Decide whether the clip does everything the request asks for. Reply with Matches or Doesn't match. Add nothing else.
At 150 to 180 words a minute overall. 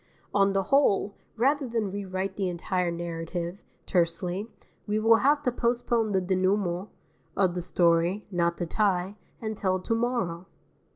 Doesn't match